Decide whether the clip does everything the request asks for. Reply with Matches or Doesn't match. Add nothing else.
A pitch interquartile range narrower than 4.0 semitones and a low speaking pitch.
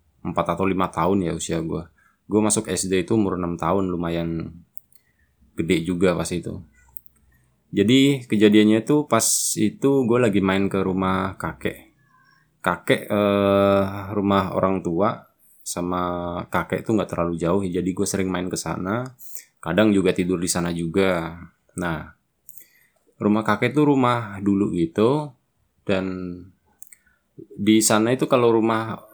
Matches